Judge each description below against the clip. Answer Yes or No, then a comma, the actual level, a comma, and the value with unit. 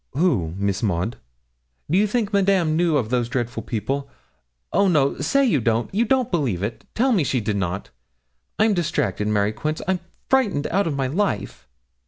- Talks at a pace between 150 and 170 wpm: No, average, 180 wpm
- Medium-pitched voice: Yes, medium, 145 Hz